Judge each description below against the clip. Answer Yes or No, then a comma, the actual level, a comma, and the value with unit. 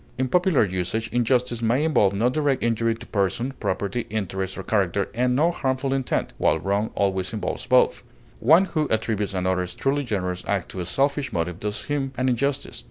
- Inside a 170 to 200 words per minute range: Yes, average, 180 wpm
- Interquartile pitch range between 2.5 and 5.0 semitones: No, wide, 5.5 semitones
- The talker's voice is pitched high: No, low, 115 Hz